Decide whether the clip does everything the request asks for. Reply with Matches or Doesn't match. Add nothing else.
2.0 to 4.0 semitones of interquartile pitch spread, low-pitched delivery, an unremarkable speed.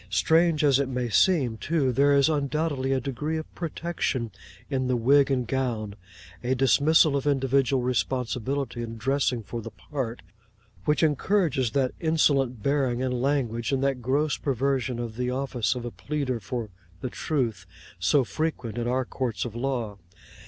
Matches